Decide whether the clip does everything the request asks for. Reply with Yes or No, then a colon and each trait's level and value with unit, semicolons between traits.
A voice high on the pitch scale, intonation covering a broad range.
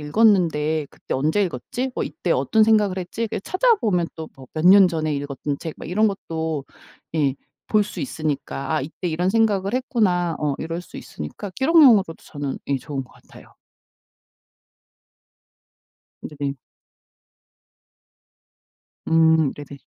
No: medium, 165 Hz; wide, 5.8 semitones